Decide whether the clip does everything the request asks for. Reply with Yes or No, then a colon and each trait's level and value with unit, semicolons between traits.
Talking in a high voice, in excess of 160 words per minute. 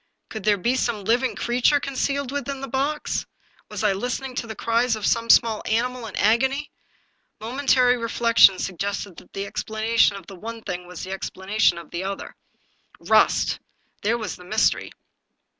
Yes: high, 230 Hz; average, 170 wpm